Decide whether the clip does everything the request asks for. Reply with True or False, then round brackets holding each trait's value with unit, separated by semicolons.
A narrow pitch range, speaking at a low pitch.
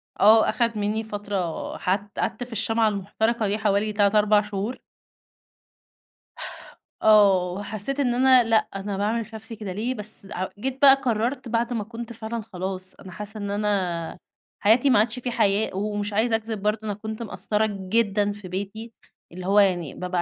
False (2.2 semitones; 210 Hz)